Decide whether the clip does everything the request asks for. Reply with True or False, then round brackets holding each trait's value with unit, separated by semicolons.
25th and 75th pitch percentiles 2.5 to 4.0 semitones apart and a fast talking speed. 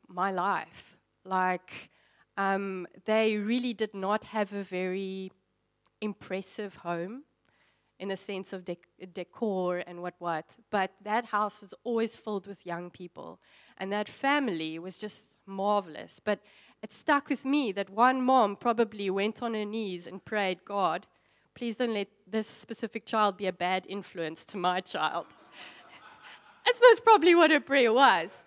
False (3.3 semitones; 155 wpm)